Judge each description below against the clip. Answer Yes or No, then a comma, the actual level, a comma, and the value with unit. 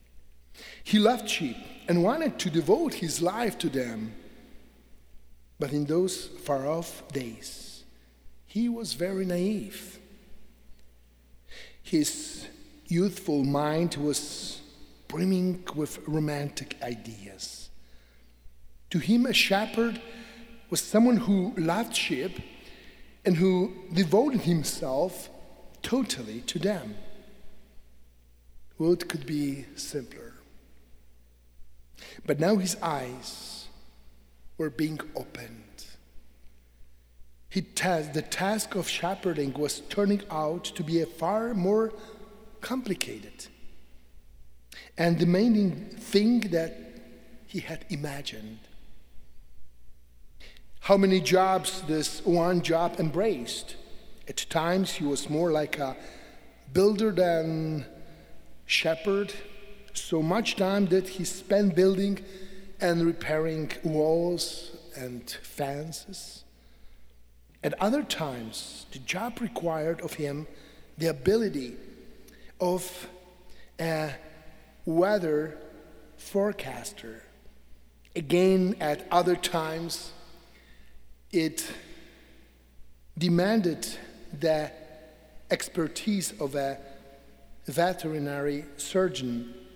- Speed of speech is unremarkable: No, slow, 90 wpm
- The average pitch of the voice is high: No, medium, 160 Hz